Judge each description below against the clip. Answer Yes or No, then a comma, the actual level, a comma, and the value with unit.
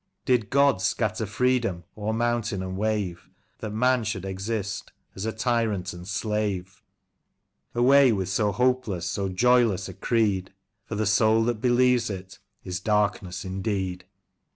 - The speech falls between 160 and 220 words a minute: No, average, 140 wpm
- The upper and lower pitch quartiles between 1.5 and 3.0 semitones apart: No, average, 3.7 semitones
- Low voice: Yes, low, 105 Hz